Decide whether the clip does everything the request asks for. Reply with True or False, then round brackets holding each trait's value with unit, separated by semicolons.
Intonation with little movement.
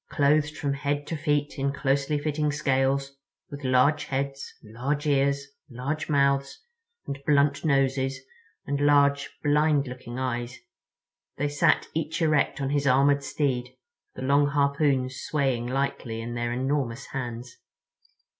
True (1.7 semitones)